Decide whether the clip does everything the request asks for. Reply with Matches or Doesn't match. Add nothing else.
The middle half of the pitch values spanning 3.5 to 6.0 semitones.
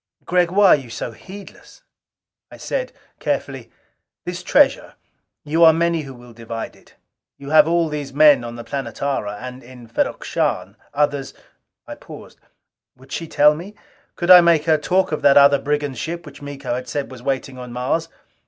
Matches